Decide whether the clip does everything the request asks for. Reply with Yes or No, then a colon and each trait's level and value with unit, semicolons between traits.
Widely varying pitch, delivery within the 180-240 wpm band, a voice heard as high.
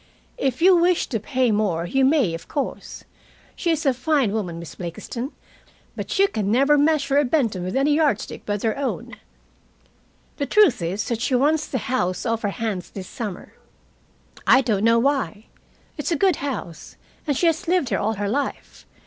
Yes: wide, 6.1 semitones; average, 190 wpm; very high, 255 Hz